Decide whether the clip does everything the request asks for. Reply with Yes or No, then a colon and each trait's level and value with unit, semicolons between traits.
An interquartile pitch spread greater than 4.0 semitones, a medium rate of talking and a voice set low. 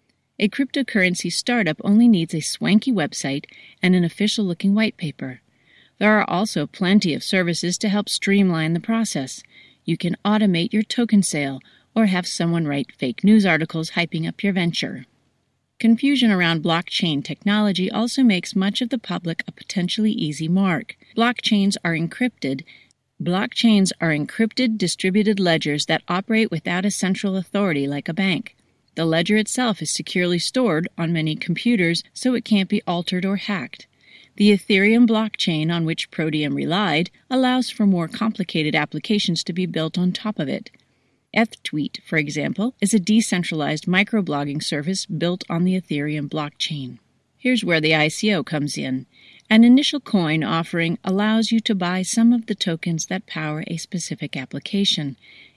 No: average, 4.8 semitones; average, 155 wpm; medium, 185 Hz